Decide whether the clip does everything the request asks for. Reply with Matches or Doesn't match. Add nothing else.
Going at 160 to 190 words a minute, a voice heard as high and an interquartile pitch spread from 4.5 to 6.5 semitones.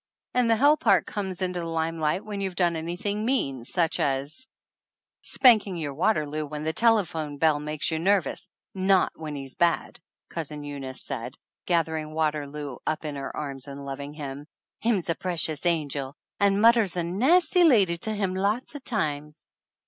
Doesn't match